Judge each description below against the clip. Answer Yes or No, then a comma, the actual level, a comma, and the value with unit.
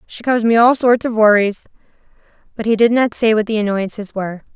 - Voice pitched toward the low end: No, high, 220 Hz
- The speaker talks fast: Yes, fast, 210 wpm